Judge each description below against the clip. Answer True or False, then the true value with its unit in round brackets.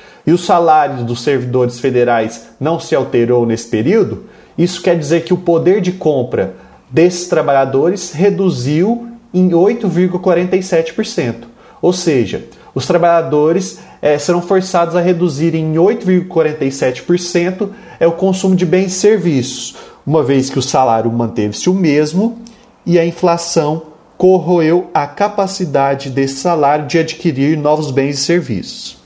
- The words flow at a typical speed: True (130 wpm)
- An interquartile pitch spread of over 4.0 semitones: True (4.6 semitones)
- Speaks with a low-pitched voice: False (170 Hz)